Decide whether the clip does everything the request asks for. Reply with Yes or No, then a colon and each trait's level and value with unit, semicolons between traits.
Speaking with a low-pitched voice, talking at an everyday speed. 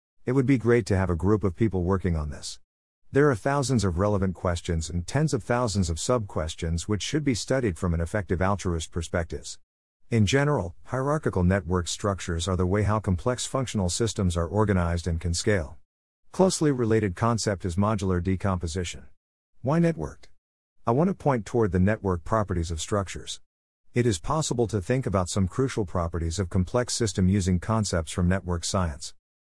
Yes: very low, 95 Hz; average, 175 wpm